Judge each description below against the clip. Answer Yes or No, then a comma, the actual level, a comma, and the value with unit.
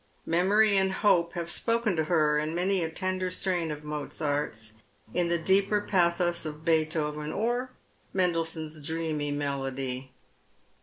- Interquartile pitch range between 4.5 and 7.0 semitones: No, average, 3.7 semitones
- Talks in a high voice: No, medium, 165 Hz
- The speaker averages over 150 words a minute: No, slow, 135 wpm